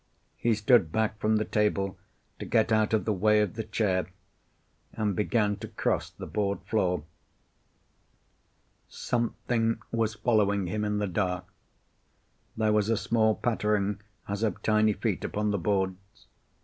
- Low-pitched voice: Yes, low, 105 Hz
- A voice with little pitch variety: Yes, narrow, 1.6 semitones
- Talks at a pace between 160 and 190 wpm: No, average, 150 wpm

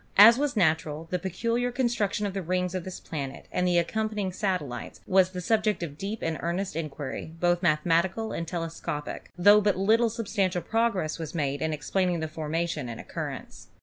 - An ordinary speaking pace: Yes, average, 190 wpm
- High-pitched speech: No, medium, 180 Hz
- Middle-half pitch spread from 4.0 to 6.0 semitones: Yes, average, 4.3 semitones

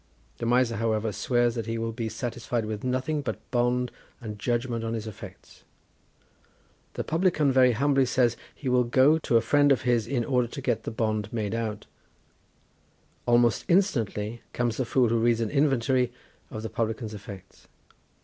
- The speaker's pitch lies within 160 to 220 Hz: No, low, 120 Hz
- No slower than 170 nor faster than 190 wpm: Yes, average, 175 wpm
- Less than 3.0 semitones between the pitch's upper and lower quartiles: Yes, narrow, 2.4 semitones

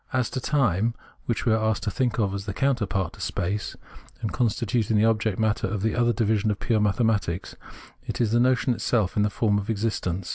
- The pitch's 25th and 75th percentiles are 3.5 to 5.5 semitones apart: No, narrow, 2.4 semitones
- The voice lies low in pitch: Yes, low, 110 Hz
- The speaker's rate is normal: No, fast, 220 wpm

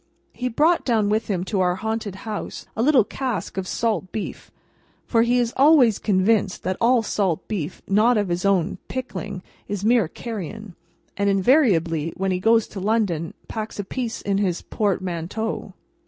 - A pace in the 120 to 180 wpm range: Yes, average, 170 wpm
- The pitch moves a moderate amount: Yes, average, 3.5 semitones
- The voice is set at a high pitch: Yes, high, 205 Hz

